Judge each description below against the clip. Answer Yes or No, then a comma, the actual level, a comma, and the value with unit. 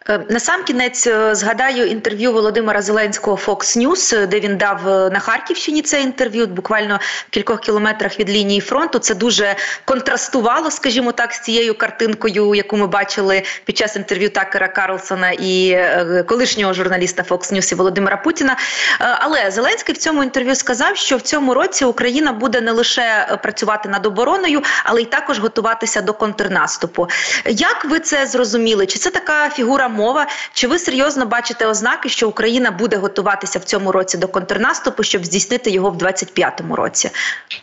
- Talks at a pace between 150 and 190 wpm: Yes, fast, 155 wpm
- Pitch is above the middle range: Yes, high, 225 Hz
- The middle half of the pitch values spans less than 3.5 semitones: No, average, 4.5 semitones